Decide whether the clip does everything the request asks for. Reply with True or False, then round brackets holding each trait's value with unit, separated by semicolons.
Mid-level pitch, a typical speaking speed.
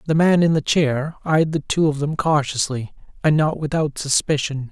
True (150 Hz; 190 wpm)